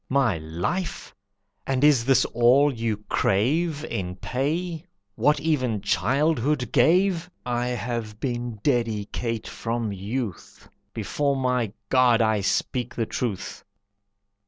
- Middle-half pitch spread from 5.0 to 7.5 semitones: No, average, 4.2 semitones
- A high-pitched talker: No, low, 125 Hz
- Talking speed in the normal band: No, slow, 110 wpm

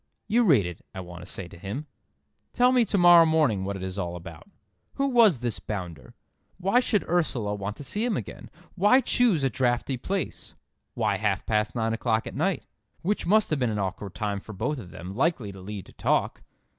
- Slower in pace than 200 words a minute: No, fast, 205 wpm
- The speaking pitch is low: Yes, low, 115 Hz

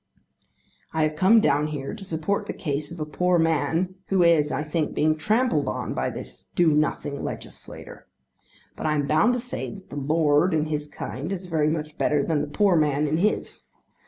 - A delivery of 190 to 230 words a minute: Yes, average, 200 wpm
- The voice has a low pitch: No, medium, 155 Hz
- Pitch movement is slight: No, average, 3.2 semitones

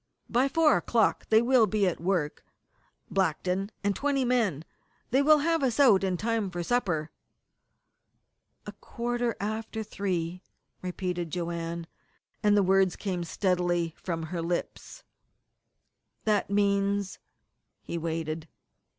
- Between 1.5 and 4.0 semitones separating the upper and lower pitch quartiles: No, average, 4.8 semitones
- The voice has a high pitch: Yes, high, 195 Hz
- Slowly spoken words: Yes, slow, 125 wpm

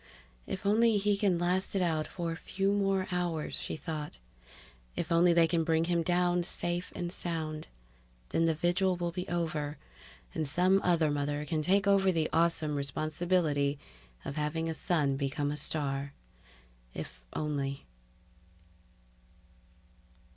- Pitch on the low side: No, medium, 165 Hz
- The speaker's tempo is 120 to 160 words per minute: Yes, average, 145 wpm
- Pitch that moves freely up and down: No, average, 2.9 semitones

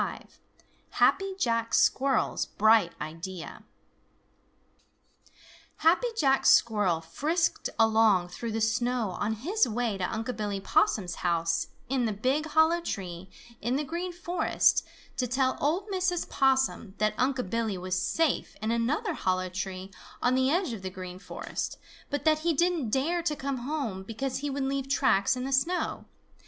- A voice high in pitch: Yes, high, 245 Hz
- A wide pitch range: Yes, wide, 6.6 semitones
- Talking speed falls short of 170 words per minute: Yes, average, 155 wpm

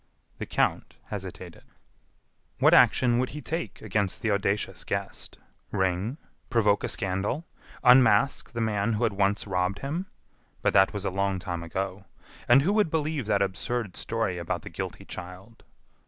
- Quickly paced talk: No, average, 155 wpm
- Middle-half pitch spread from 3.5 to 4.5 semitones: Yes, average, 4.1 semitones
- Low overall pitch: Yes, low, 105 Hz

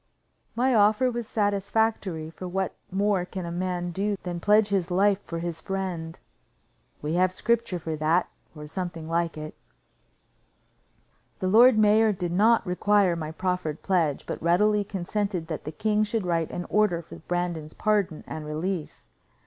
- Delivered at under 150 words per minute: No, average, 155 wpm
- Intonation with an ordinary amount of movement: Yes, average, 3.7 semitones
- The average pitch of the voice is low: No, medium, 185 Hz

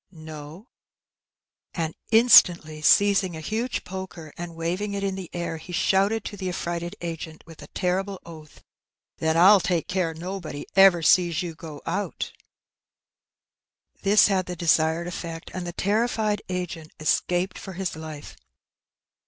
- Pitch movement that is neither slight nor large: Yes, average, 3.0 semitones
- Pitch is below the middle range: No, medium, 175 Hz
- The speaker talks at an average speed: Yes, average, 150 wpm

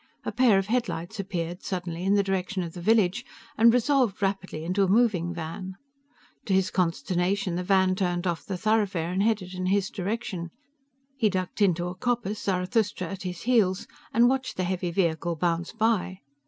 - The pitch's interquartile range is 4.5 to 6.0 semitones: No, average, 2.9 semitones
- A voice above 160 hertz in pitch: Yes, high, 190 Hz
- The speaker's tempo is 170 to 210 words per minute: Yes, average, 180 wpm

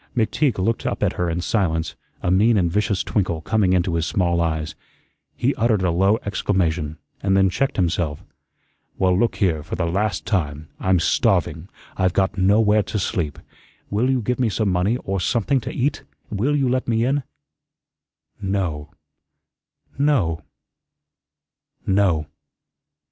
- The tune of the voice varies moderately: Yes, average, 4.4 semitones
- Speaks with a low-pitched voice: Yes, very low, 95 Hz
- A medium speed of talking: Yes, average, 150 wpm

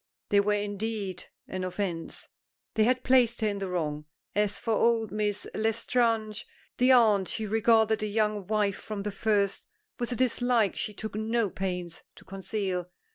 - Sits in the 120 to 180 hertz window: No, high, 210 Hz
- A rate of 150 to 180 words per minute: Yes, average, 165 wpm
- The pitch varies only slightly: Yes, narrow, 2.3 semitones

